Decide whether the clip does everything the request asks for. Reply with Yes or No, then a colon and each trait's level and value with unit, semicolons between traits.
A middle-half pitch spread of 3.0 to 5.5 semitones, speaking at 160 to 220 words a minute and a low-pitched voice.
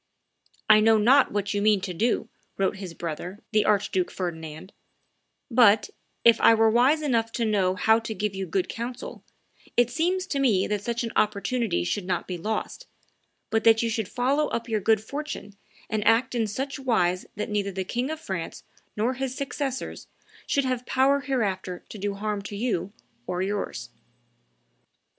No: average, 3.9 semitones; average, 175 wpm; high, 220 Hz